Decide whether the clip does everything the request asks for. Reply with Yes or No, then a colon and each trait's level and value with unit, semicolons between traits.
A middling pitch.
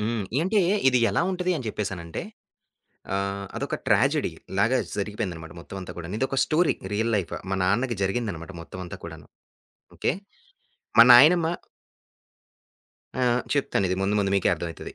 No: low, 100 Hz